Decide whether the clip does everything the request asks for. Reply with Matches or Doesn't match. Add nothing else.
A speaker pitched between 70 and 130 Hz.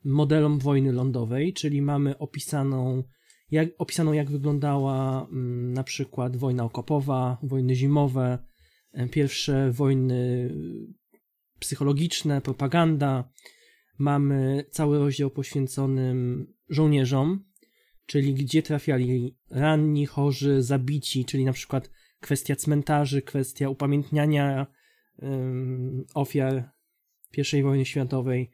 Doesn't match